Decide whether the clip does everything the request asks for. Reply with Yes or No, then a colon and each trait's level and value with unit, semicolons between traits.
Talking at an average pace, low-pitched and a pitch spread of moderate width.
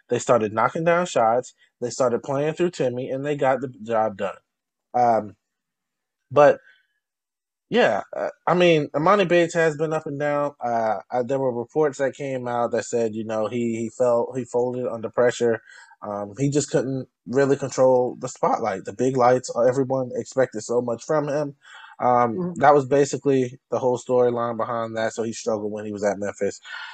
Yes: average, 180 wpm; low, 125 Hz; average, 3.5 semitones